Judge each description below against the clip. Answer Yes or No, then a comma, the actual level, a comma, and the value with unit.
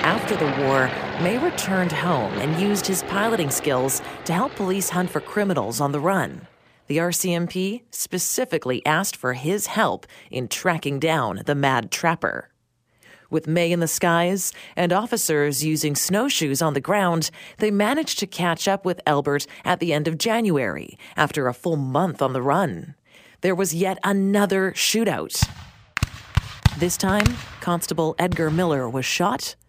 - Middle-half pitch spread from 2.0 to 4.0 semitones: No, average, 4.5 semitones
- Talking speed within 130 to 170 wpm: Yes, average, 155 wpm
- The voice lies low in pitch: No, medium, 175 Hz